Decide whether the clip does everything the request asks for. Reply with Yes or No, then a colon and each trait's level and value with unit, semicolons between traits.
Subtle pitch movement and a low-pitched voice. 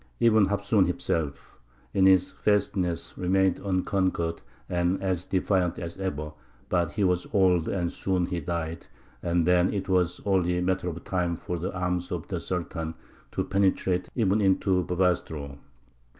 Yes: narrow, 1.8 semitones; very low, 90 Hz